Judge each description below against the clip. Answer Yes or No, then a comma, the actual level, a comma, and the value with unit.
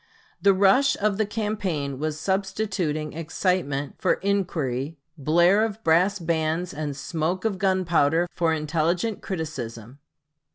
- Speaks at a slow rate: Yes, slow, 120 wpm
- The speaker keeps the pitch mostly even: No, average, 4.2 semitones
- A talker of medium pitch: Yes, medium, 170 Hz